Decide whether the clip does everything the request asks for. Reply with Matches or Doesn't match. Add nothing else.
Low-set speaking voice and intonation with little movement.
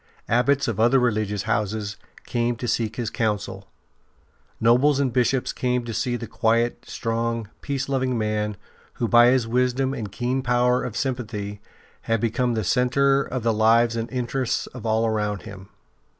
Matches